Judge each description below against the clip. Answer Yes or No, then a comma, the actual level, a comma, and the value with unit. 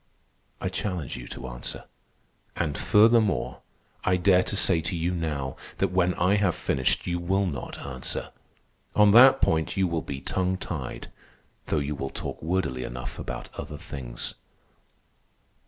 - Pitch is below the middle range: Yes, very low, 85 Hz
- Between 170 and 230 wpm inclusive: No, average, 155 wpm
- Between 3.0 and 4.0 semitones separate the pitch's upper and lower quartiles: No, average, 5.0 semitones